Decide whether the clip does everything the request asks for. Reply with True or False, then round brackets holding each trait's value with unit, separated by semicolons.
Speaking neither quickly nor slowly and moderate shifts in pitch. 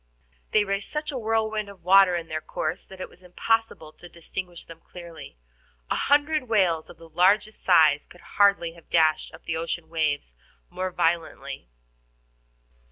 True (165 wpm; 3.9 semitones)